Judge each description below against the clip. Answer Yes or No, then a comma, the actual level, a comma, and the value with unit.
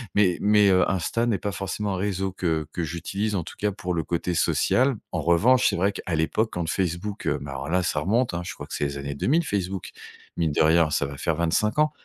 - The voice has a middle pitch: No, very low, 90 Hz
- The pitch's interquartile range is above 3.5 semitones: Yes, average, 4.0 semitones